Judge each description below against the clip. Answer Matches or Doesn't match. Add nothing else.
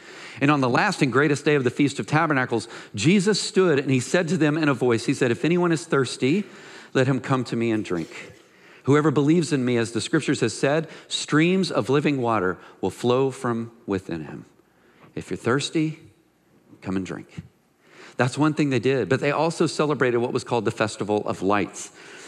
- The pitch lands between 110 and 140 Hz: Matches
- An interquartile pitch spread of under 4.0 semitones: Doesn't match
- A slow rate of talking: Doesn't match